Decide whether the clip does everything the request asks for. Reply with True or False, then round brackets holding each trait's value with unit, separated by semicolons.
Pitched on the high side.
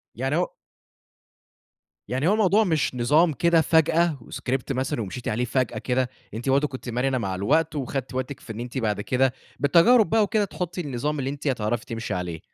False (135 Hz)